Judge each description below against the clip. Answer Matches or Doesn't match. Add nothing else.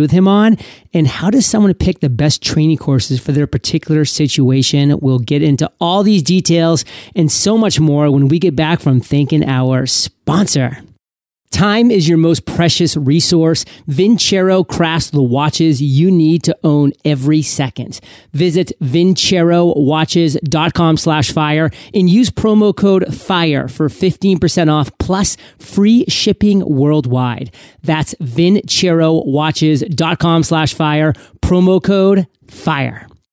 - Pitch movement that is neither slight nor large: Matches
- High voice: Doesn't match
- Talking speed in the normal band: Doesn't match